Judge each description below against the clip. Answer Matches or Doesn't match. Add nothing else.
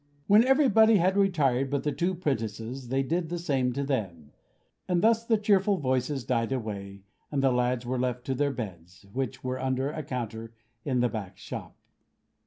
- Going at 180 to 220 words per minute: Matches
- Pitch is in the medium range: Doesn't match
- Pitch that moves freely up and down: Matches